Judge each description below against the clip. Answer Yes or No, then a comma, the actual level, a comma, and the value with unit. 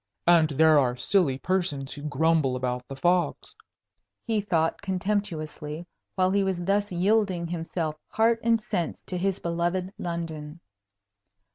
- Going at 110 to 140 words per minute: Yes, slow, 135 wpm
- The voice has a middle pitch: Yes, medium, 170 Hz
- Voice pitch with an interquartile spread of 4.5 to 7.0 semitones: No, average, 3.8 semitones